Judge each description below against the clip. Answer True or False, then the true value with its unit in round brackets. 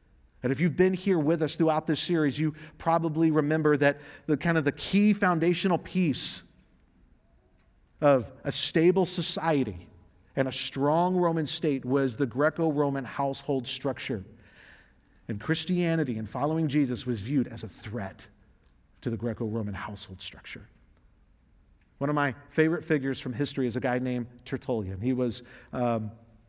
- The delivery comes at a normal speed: True (145 wpm)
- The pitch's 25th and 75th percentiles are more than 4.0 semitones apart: True (5.5 semitones)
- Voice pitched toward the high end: False (140 Hz)